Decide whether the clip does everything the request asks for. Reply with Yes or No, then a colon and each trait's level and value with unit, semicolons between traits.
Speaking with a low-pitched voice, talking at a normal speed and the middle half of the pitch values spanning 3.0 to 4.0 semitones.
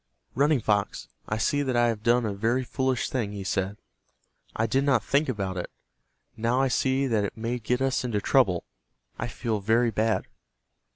Yes: low, 115 Hz; average, 185 wpm; average, 3.6 semitones